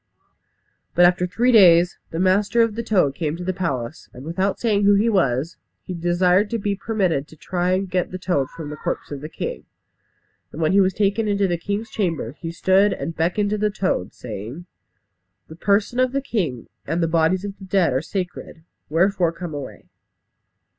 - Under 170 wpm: No, average, 200 wpm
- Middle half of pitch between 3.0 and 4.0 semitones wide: Yes, average, 3.7 semitones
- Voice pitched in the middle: Yes, medium, 180 Hz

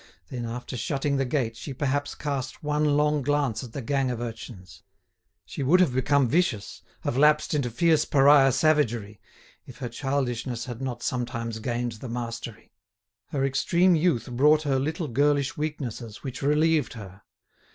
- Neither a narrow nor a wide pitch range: Yes, average, 3.7 semitones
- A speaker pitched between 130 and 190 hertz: Yes, low, 135 Hz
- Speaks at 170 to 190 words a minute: No, average, 160 wpm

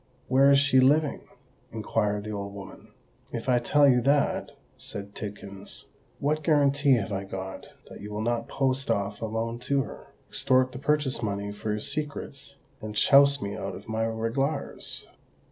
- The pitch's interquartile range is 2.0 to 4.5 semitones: No, average, 5.1 semitones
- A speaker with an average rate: Yes, average, 165 wpm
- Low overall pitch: Yes, low, 120 Hz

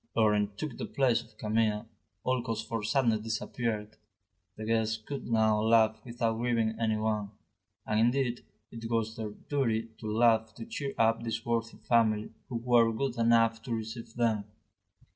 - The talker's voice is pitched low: Yes, low, 115 Hz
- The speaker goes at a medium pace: Yes, average, 160 wpm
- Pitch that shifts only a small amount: Yes, narrow, 1.3 semitones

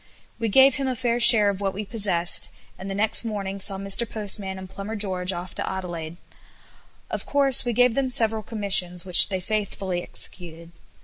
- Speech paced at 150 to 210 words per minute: Yes, average, 185 wpm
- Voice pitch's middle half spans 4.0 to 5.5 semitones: No, average, 3.2 semitones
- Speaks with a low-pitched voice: No, high, 200 Hz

